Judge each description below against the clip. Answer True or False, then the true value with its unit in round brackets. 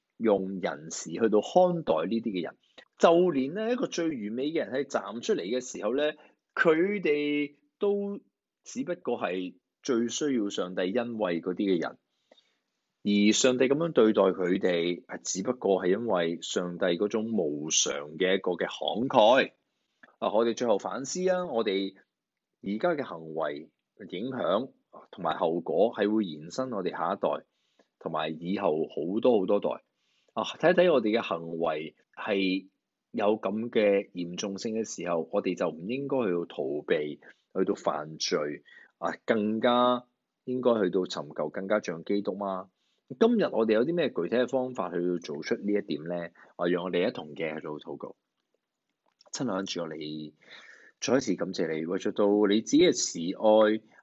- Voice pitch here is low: True (105 Hz)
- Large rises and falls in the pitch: True (6.2 semitones)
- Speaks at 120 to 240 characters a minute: True (235 characters per minute)